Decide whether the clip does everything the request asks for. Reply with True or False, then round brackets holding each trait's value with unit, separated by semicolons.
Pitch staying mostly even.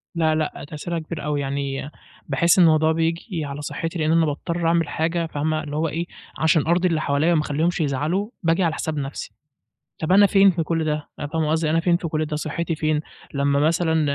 True (1.9 semitones)